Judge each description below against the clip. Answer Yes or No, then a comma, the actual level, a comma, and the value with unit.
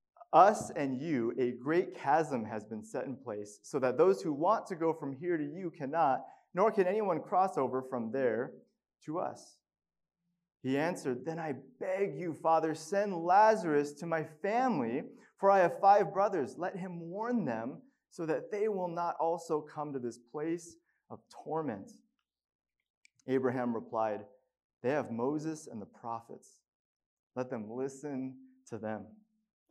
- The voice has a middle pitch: Yes, medium, 160 Hz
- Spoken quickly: No, average, 160 wpm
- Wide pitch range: Yes, wide, 6.2 semitones